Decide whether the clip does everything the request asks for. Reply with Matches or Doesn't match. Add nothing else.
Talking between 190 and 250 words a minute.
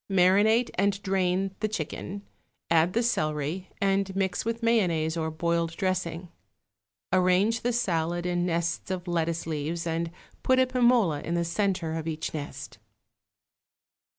Doesn't match